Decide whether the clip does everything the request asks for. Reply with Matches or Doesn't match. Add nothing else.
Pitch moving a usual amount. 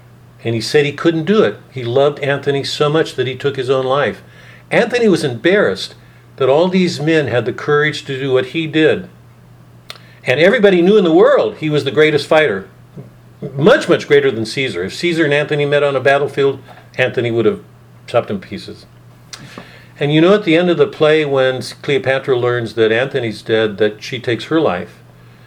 Matches